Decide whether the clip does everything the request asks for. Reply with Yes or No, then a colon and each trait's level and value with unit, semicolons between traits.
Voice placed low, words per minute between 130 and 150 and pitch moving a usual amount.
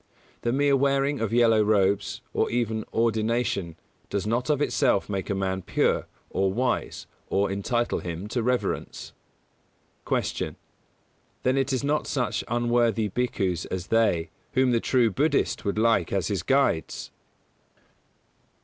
Yes: low, 115 Hz; average, 140 wpm; average, 4.2 semitones